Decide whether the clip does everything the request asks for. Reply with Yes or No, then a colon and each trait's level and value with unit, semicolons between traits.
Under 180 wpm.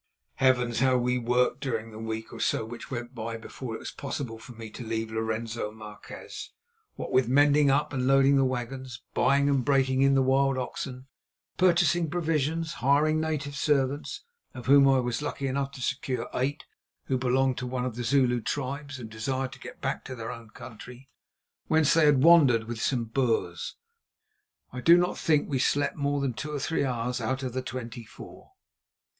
No: average, 190 wpm